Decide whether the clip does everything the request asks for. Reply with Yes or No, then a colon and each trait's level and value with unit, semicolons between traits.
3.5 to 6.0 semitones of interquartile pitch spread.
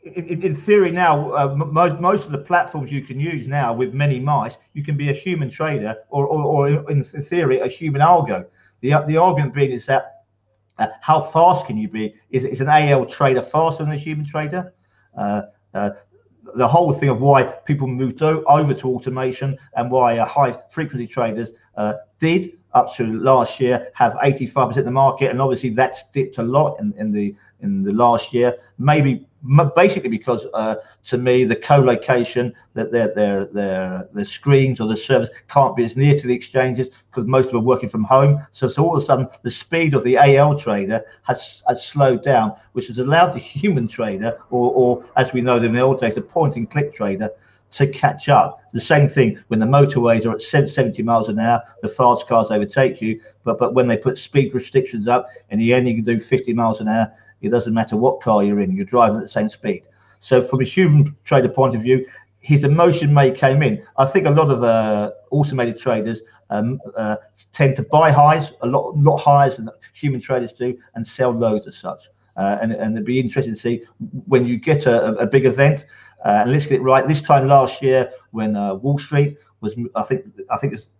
Yes: average, 3.9 semitones